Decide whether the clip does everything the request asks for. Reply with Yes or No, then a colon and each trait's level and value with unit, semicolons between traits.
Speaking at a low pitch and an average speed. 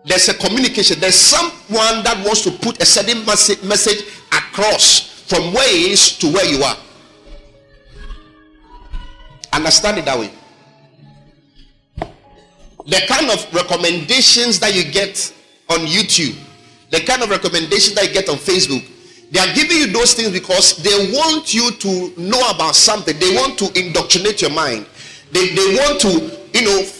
No: high, 195 Hz; average, 150 wpm